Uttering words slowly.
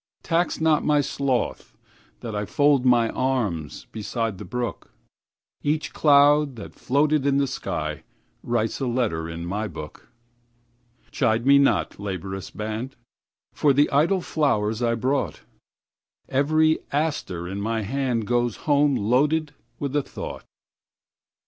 Yes: slow, 110 wpm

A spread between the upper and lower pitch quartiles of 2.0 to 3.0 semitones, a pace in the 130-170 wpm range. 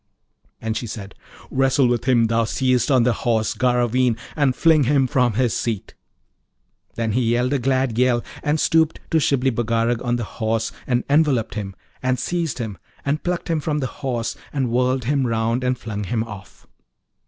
No: average, 2.7 semitones; average, 180 wpm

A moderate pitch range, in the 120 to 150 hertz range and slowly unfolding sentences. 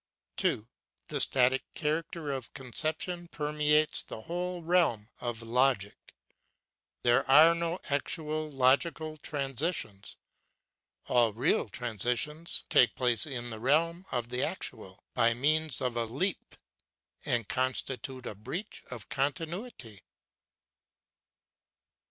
Yes: average, 4.8 semitones; low, 135 Hz; slow, 110 wpm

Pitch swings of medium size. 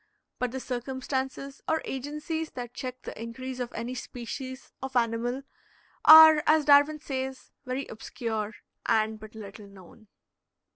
Yes: average, 3.1 semitones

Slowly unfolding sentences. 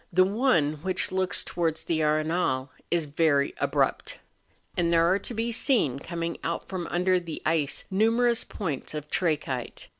No: average, 155 wpm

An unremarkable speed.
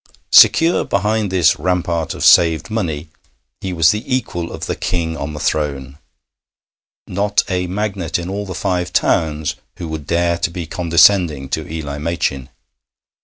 Yes: average, 155 wpm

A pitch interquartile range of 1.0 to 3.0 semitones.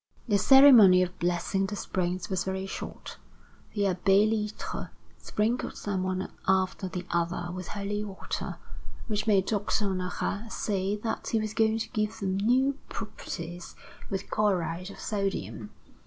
Yes: narrow, 2.5 semitones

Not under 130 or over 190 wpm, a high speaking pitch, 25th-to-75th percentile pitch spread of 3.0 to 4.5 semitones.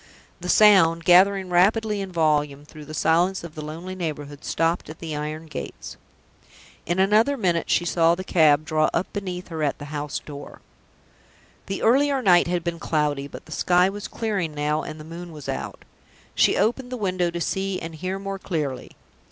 No: average, 185 wpm; medium, 170 Hz; average, 3.8 semitones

